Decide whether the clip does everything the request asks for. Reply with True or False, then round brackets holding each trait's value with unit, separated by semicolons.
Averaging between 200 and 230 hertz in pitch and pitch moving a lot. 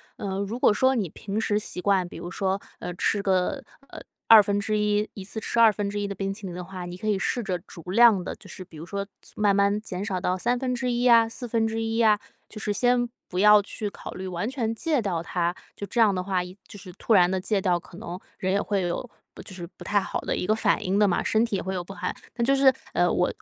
False (205 Hz; 3.2 semitones)